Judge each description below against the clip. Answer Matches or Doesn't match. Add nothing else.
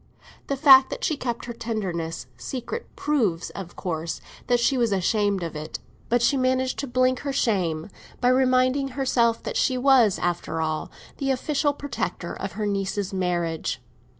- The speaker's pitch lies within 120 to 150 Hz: Doesn't match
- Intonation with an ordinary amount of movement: Doesn't match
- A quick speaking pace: Doesn't match